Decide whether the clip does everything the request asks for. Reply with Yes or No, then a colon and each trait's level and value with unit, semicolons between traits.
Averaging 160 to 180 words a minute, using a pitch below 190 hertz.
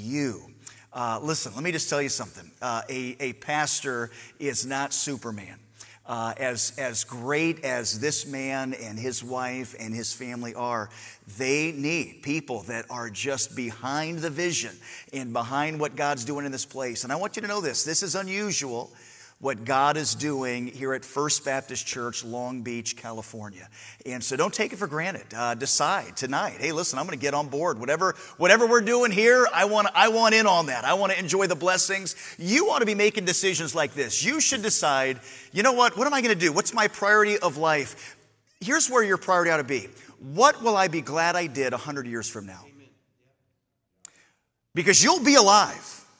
No: average, 195 wpm; medium, 140 Hz